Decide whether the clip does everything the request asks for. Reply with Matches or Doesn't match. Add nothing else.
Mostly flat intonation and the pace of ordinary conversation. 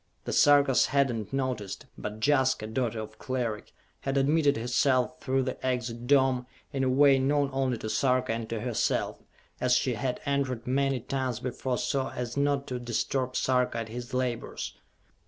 Matches